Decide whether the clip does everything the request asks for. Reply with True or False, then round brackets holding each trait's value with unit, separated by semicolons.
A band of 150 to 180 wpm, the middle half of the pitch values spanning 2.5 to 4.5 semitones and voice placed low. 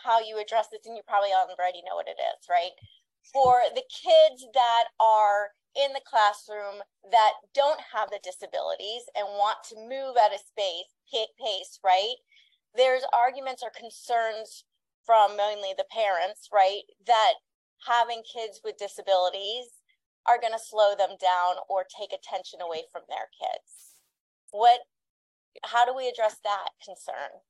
False (155 wpm; 3.6 semitones; 220 Hz)